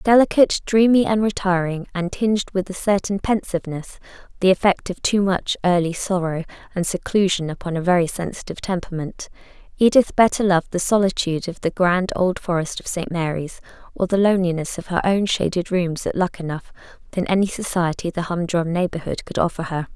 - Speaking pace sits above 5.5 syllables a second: Yes, 5.7 syllables/s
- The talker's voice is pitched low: No, medium, 185 Hz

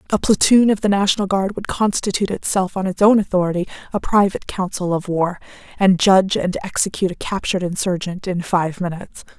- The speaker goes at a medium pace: Yes, average, 180 wpm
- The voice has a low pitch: No, high, 190 Hz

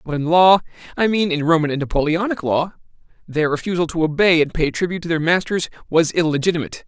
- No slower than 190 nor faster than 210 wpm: No, average, 175 wpm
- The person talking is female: No, male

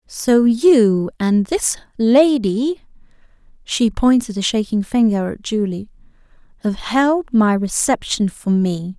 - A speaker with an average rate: No, slow, 105 wpm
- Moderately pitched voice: No, high, 230 Hz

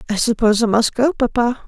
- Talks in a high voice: Yes, high, 235 Hz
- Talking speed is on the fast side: Yes, fast, 215 wpm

